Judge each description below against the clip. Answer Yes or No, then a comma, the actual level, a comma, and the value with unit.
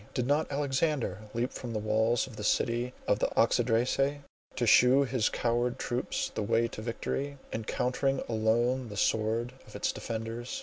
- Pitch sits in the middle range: No, low, 120 Hz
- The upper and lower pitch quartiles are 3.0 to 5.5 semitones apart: No, narrow, 2.6 semitones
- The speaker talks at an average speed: Yes, average, 165 wpm